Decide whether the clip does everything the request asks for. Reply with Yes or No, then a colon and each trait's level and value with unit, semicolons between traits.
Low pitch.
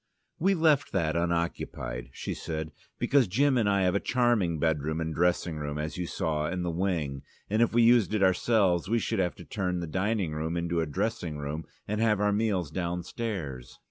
Yes: very low, 90 Hz